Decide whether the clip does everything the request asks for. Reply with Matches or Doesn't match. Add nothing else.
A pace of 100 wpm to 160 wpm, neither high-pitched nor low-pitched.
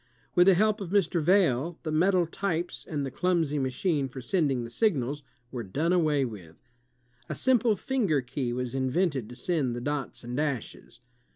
Doesn't match